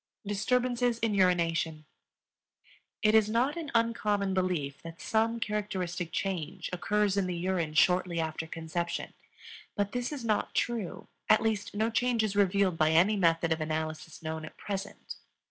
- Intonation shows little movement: No, average, 4.6 semitones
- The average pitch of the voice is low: No, high, 195 Hz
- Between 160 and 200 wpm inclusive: No, average, 150 wpm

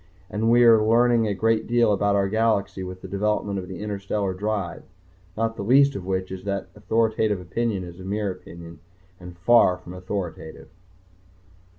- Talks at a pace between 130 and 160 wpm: No, average, 170 wpm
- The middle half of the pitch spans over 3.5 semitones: No, average, 3.2 semitones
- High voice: No, low, 100 Hz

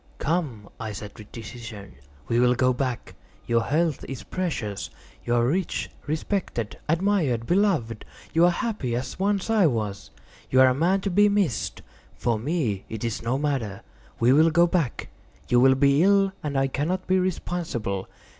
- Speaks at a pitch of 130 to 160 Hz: Yes, low, 135 Hz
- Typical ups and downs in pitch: No, wide, 7.1 semitones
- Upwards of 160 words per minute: Yes, average, 170 wpm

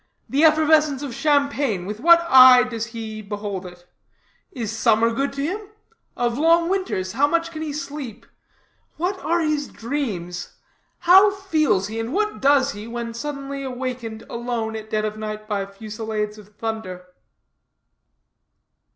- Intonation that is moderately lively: No, wide, 5.8 semitones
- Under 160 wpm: Yes, average, 150 wpm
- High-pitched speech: Yes, high, 245 Hz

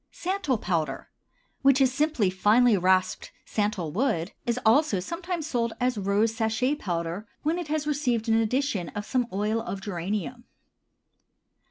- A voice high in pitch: Yes, high, 225 Hz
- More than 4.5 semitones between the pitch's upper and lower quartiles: Yes, wide, 5.6 semitones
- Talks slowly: No, average, 145 wpm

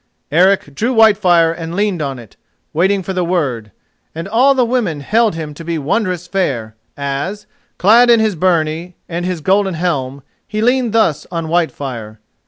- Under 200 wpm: Yes, average, 170 wpm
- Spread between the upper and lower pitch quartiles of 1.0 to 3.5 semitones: No, average, 5.1 semitones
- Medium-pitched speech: Yes, medium, 175 Hz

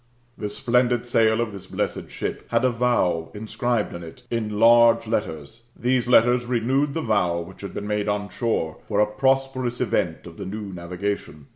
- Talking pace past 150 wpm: Yes, average, 180 wpm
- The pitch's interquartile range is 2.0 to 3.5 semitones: Yes, average, 3.2 semitones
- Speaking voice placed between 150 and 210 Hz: No, low, 110 Hz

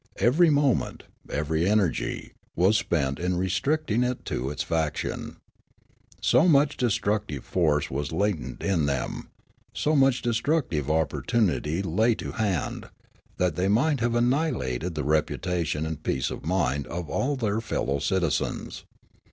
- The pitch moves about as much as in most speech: No, wide, 7.5 semitones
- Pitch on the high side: No, very low, 95 Hz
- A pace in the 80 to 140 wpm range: Yes, slow, 135 wpm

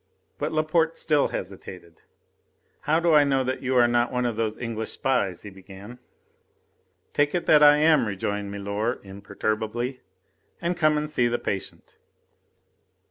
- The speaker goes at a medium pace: Yes, average, 150 wpm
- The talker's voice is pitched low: Yes, low, 120 Hz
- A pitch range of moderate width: No, wide, 6.6 semitones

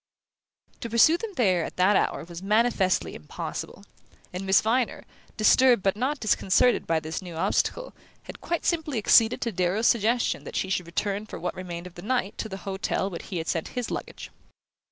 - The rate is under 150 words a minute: No, average, 190 wpm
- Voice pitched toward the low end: No, high, 200 Hz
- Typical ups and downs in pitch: Yes, average, 4.7 semitones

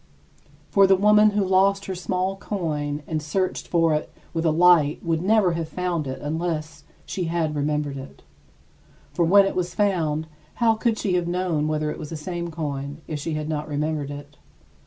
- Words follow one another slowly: No, average, 190 wpm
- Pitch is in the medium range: Yes, medium, 165 Hz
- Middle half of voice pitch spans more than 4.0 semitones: No, average, 3.5 semitones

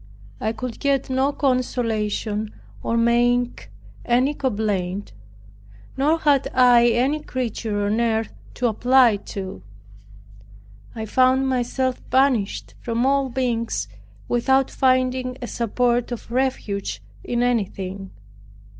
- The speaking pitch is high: Yes, high, 245 Hz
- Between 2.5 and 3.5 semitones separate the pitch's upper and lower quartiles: Yes, average, 2.9 semitones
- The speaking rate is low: Yes, slow, 110 wpm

